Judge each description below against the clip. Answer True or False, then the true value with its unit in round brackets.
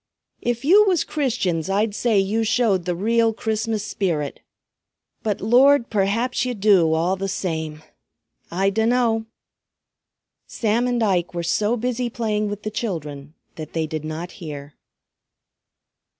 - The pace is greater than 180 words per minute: False (135 wpm)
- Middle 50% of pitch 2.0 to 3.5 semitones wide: False (5.2 semitones)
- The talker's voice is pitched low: False (210 Hz)